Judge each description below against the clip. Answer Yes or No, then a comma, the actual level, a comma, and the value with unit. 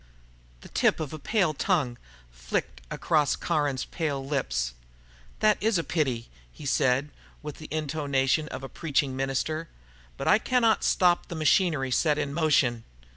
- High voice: No, medium, 150 Hz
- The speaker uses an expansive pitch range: No, average, 3.5 semitones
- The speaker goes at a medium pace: Yes, average, 150 wpm